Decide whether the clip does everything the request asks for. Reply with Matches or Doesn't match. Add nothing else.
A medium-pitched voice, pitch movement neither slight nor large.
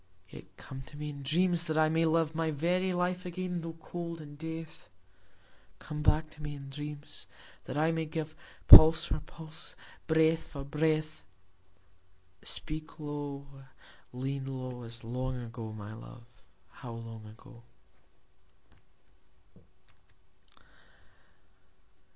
Matches